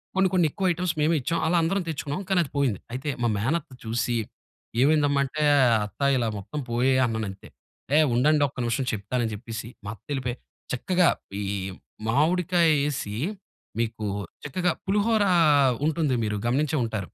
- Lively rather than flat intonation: Yes, wide, 5.8 semitones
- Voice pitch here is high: No, medium, 140 Hz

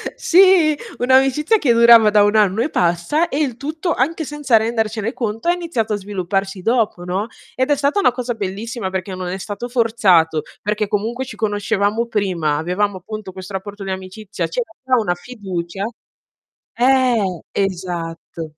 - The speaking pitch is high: Yes, high, 215 Hz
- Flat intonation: No, average, 4.9 semitones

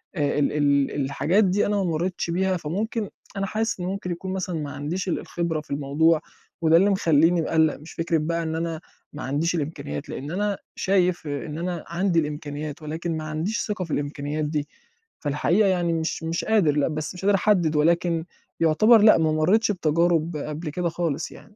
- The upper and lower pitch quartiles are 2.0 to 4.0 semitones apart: Yes, average, 3.2 semitones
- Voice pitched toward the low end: No, medium, 165 Hz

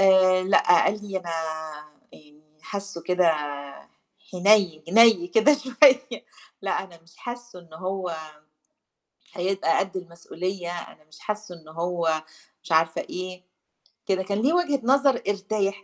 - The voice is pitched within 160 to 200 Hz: Yes, medium, 185 Hz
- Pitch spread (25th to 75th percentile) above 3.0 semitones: Yes, average, 3.6 semitones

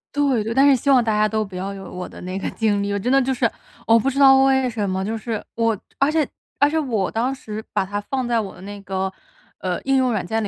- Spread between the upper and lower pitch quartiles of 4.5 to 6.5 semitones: Yes, average, 4.8 semitones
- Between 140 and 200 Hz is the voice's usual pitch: No, high, 225 Hz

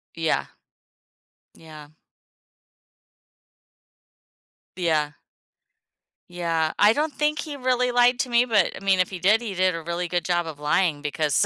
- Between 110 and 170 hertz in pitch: No, medium, 180 Hz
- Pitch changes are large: Yes, wide, 6.9 semitones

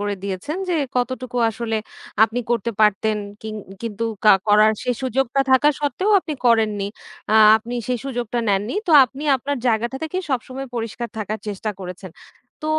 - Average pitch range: Yes, average, 3.4 semitones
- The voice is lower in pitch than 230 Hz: No, high, 235 Hz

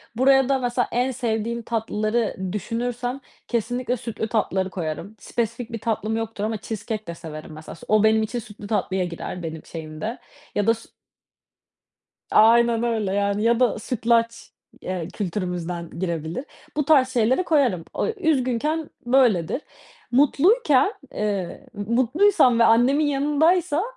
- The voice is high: Yes, high, 230 Hz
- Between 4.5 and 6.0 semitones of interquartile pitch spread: No, average, 4.0 semitones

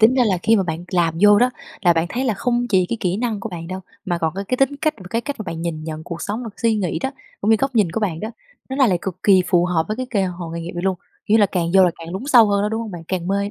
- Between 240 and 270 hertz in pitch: No, high, 195 Hz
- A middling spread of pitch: Yes, average, 4.5 semitones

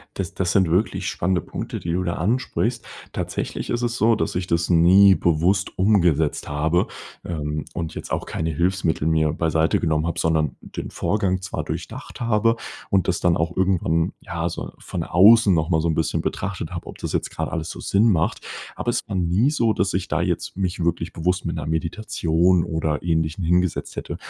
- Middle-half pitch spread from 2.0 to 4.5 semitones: Yes, average, 2.8 semitones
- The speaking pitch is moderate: No, very low, 85 Hz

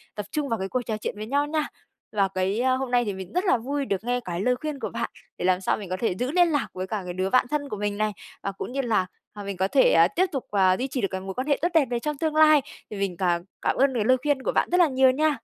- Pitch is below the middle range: No, high, 240 Hz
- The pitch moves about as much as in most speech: No, wide, 6.3 semitones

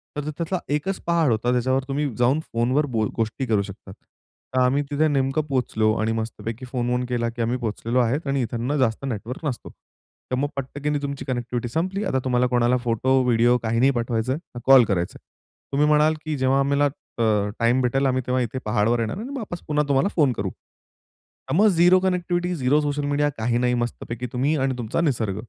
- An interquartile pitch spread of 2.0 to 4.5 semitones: Yes, average, 3.6 semitones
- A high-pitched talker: No, low, 130 Hz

